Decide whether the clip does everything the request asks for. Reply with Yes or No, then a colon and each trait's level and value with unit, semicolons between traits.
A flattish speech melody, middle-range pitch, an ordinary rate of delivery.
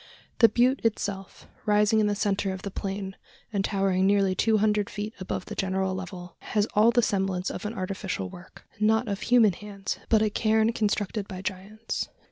No: narrow, 2.2 semitones; high, 205 Hz; average, 185 wpm